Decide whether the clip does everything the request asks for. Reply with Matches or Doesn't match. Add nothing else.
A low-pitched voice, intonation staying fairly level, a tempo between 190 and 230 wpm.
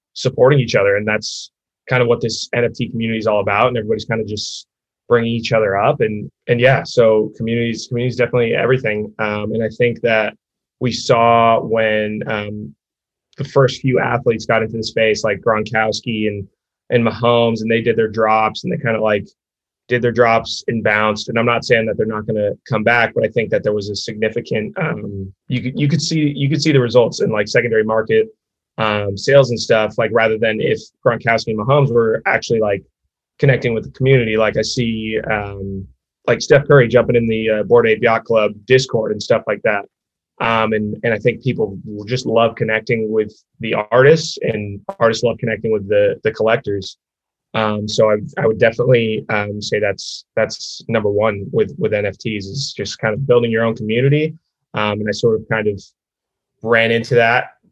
Matches